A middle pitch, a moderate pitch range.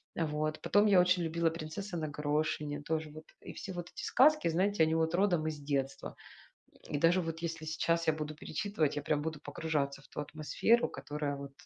No: medium, 155 Hz; narrow, 2.2 semitones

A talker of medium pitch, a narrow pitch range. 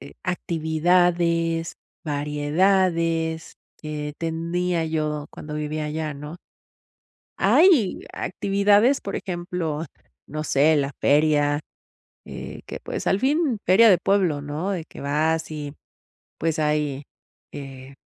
No: medium, 160 Hz; average, 3.1 semitones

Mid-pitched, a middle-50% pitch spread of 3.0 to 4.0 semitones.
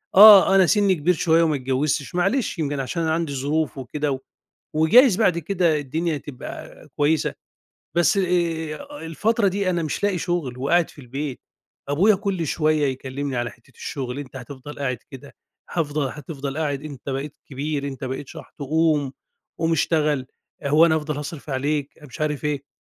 Yes: medium, 150 Hz; average, 3.5 semitones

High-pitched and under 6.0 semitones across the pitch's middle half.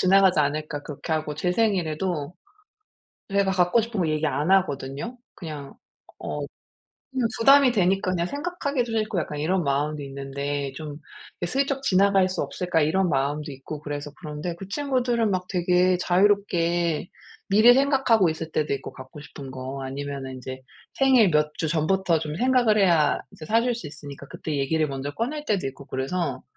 No: medium, 170 Hz; wide, 5.5 semitones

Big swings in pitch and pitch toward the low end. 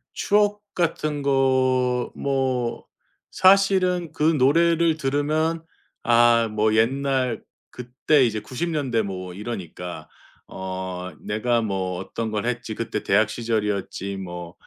Yes: wide, 5.7 semitones; low, 125 Hz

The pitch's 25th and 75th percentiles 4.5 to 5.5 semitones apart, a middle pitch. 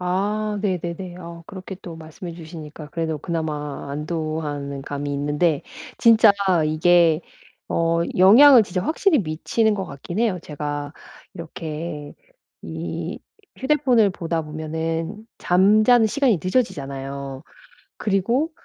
Yes: average, 5.1 semitones; medium, 170 Hz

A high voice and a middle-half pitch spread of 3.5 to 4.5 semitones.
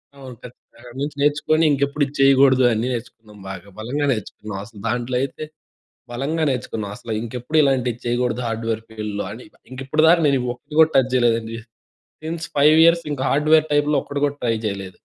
No: low, 130 Hz; average, 4.2 semitones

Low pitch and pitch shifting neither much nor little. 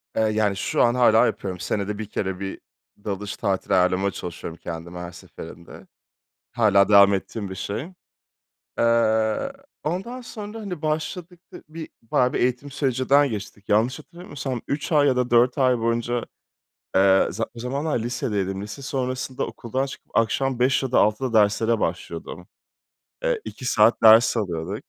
Yes: low, 115 Hz; average, 5.0 semitones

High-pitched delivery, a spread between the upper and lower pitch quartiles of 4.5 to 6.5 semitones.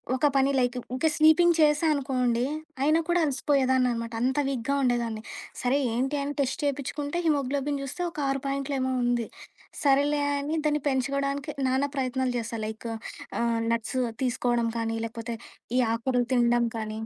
No: very high, 260 Hz; average, 2.9 semitones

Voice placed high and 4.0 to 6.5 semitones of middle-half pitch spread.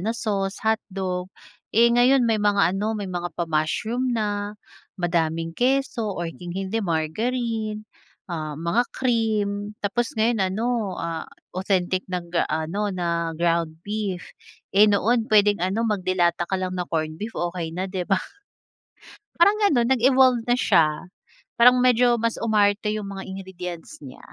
Yes: high, 200 Hz; average, 4.3 semitones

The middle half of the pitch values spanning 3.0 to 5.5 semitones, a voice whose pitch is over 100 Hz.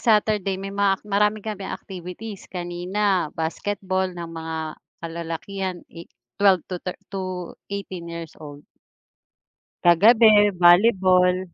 No: narrow, 2.6 semitones; medium, 185 Hz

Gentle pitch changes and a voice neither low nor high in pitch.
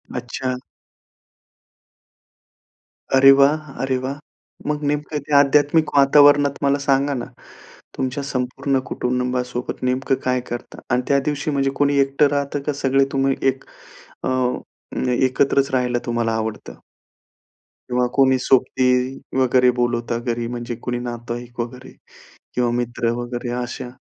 No: narrow, 2.2 semitones; low, 130 Hz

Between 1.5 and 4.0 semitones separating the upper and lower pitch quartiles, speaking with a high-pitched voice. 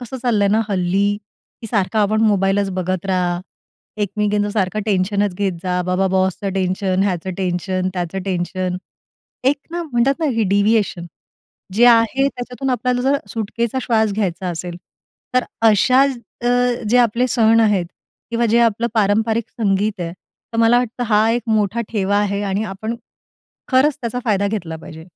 Yes: average, 3.5 semitones; high, 205 Hz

